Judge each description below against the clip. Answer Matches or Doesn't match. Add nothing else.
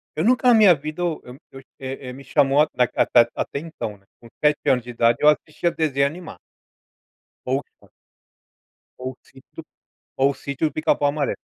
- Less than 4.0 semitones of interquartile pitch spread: Matches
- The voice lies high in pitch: Doesn't match